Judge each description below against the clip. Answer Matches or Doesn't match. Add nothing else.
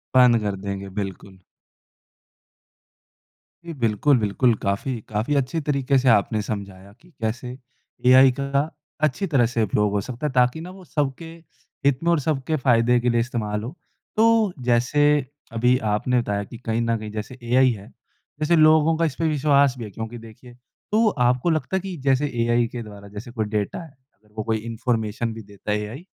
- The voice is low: Matches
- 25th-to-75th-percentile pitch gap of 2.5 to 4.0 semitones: Doesn't match